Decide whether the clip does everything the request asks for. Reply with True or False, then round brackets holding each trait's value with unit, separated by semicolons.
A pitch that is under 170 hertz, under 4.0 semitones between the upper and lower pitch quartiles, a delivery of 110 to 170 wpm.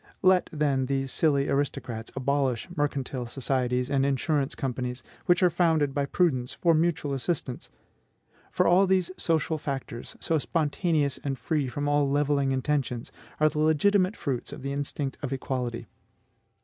True (140 Hz; 3.1 semitones; 150 wpm)